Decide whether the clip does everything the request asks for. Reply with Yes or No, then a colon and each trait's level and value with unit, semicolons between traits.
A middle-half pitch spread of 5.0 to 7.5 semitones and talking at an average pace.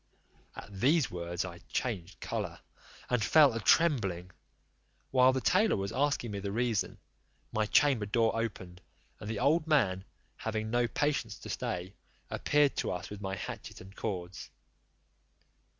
Yes: wide, 5.4 semitones; average, 150 wpm